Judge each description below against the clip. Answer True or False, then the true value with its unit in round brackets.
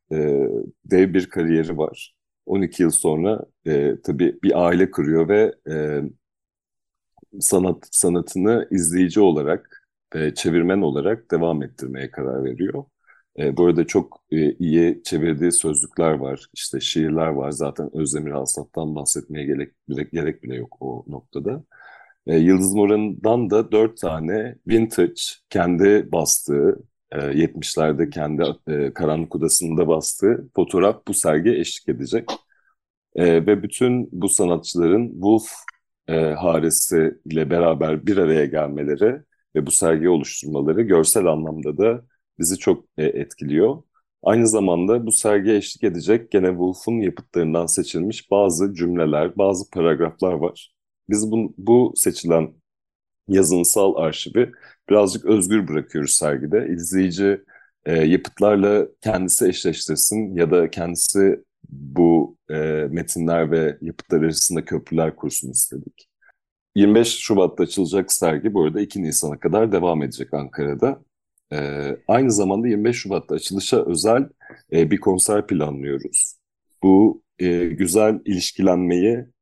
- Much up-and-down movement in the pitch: False (4.4 semitones)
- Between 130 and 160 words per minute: False (120 wpm)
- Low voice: True (85 Hz)